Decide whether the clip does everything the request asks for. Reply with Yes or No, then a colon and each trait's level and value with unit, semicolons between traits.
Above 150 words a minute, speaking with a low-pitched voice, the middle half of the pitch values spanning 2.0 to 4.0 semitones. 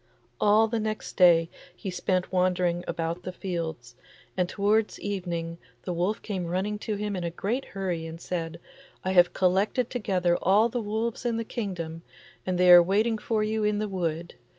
No: average, 180 wpm; medium, 185 Hz; average, 3.4 semitones